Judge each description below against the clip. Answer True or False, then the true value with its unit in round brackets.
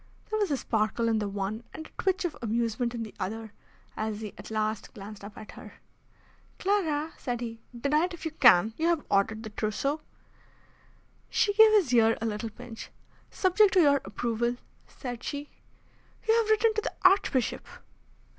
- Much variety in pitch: True (7.0 semitones)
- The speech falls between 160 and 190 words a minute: True (180 wpm)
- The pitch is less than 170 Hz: False (240 Hz)